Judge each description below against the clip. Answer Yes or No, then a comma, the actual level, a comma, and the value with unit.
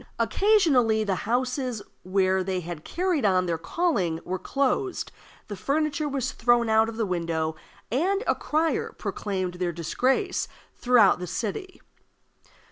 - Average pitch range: No, wide, 7.5 semitones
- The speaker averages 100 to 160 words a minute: Yes, slow, 135 wpm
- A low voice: No, high, 225 Hz